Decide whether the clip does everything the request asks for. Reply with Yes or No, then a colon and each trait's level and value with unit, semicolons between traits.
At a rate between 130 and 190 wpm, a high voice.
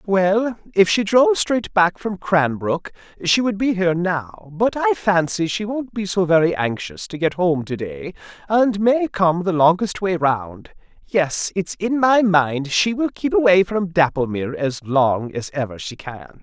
No: average, 180 wpm; medium, 180 Hz